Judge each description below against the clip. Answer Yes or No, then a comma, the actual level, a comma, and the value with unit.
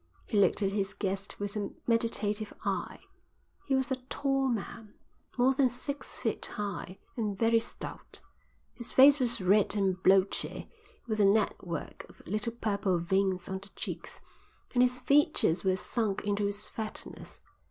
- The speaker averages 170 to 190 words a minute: No, average, 155 wpm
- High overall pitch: Yes, high, 210 Hz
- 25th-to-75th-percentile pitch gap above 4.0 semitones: No, average, 3.6 semitones